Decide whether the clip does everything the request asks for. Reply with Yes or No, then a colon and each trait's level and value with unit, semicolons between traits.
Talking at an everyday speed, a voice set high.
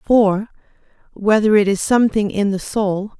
Yes: average, 150 wpm; high, 205 Hz